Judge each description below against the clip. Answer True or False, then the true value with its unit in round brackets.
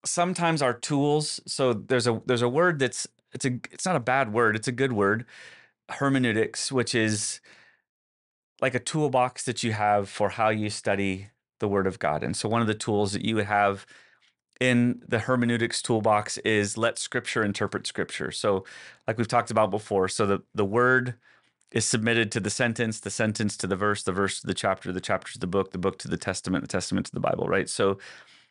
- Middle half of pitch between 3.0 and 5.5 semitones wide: True (3.4 semitones)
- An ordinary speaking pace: False (210 wpm)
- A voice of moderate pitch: False (110 Hz)